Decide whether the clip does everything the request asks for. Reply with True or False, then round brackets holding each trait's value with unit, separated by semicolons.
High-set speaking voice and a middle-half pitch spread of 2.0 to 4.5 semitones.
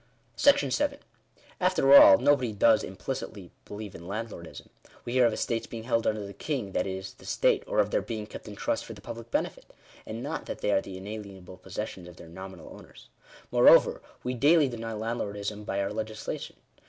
False (110 Hz; 3.4 semitones)